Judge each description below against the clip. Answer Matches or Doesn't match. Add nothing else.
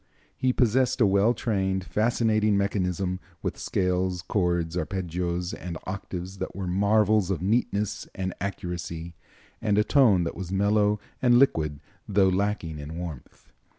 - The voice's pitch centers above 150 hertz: Doesn't match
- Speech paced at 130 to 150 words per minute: Matches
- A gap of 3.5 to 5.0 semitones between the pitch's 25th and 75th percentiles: Doesn't match